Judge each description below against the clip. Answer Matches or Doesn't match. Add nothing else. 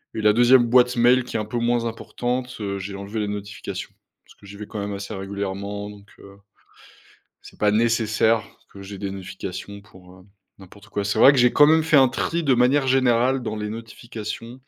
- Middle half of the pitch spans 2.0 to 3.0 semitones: Doesn't match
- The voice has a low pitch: Matches